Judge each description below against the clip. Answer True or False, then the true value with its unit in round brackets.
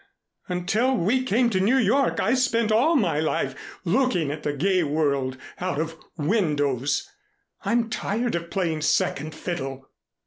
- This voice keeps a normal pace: True (150 wpm)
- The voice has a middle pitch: True (180 Hz)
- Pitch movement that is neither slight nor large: False (7.4 semitones)